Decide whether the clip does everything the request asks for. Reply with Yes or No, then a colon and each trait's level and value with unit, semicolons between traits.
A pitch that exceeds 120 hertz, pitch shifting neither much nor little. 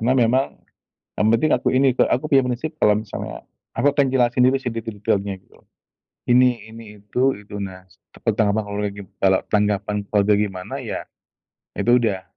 No: low, 110 Hz; average, 3.6 semitones